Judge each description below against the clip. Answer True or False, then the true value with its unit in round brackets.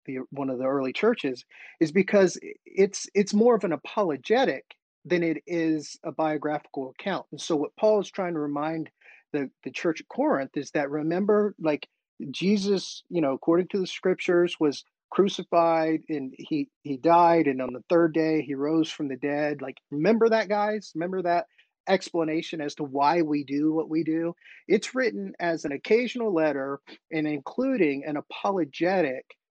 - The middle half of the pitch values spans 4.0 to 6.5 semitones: True (4.5 semitones)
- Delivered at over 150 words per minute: True (175 wpm)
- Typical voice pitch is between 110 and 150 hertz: False (160 Hz)